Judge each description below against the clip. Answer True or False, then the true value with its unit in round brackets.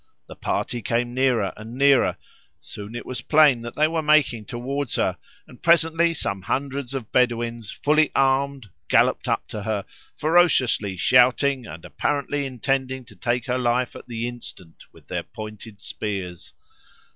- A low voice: True (125 Hz)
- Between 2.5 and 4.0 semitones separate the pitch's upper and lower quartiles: True (3.7 semitones)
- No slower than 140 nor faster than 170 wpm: True (155 wpm)